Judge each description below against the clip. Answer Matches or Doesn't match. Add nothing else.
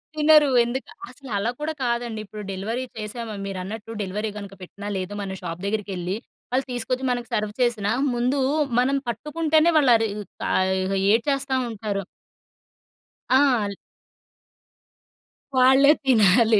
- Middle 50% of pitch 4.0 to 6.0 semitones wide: Matches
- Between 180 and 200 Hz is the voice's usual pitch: Doesn't match